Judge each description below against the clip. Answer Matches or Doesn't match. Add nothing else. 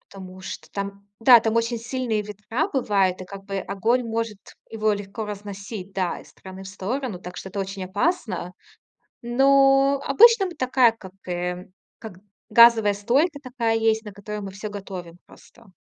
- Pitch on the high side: Matches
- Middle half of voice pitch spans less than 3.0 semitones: Doesn't match